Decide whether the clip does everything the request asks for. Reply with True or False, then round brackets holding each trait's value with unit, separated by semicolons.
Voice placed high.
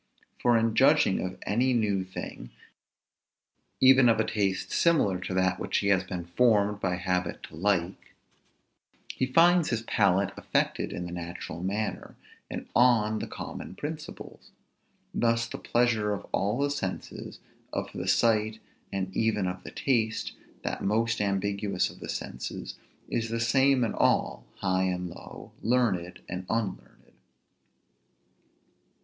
False (105 Hz)